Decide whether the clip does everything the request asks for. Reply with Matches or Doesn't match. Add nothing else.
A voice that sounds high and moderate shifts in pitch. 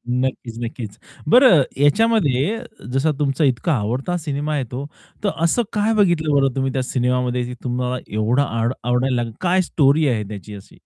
Doesn't match